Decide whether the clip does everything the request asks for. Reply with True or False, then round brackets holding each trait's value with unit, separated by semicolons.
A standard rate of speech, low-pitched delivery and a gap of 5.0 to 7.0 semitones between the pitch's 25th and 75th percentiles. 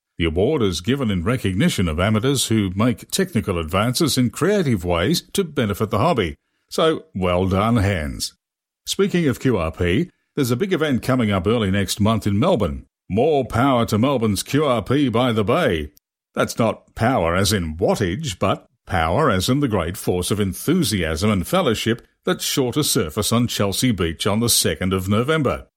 True (170 wpm; 110 Hz; 5.3 semitones)